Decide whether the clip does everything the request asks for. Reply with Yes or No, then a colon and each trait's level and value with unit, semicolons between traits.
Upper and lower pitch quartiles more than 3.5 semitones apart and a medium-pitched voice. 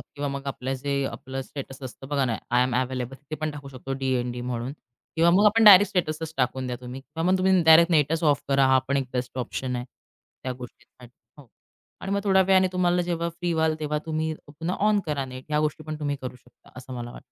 Yes: average, 4.1 semitones; medium, 145 Hz